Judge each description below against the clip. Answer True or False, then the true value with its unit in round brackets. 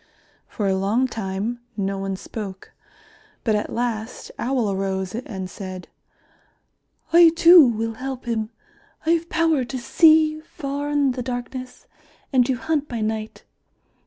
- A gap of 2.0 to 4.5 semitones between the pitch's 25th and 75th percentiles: False (5.0 semitones)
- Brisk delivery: False (140 wpm)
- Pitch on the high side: True (240 Hz)